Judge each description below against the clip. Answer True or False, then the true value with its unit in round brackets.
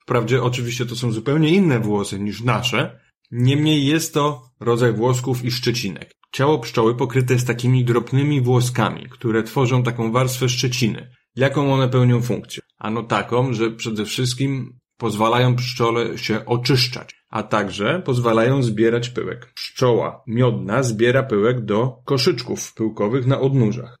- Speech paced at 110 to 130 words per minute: False (140 wpm)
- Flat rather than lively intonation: True (2.3 semitones)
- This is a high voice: False (125 Hz)